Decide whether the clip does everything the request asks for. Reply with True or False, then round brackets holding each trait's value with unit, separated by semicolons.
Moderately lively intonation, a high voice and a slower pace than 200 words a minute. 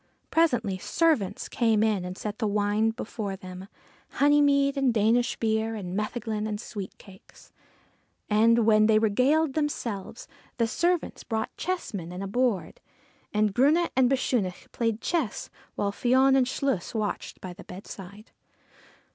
True (4.2 semitones; 220 Hz; 140 wpm)